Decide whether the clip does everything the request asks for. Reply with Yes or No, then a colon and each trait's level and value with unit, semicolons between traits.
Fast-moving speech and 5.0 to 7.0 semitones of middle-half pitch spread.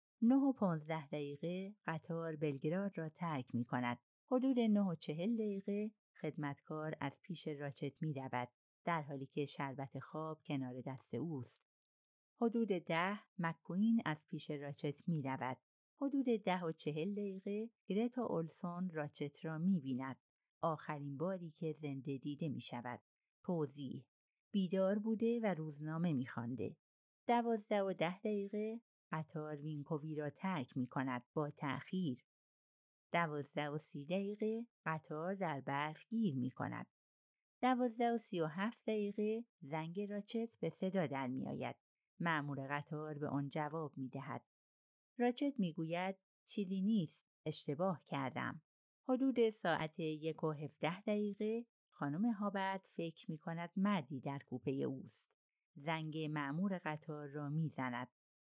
No: average, 130 wpm; wide, 5.6 semitones